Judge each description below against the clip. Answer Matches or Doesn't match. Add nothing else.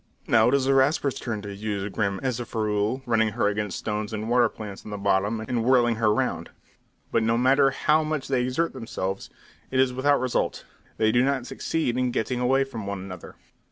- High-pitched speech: Doesn't match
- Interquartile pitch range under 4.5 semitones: Matches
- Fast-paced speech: Matches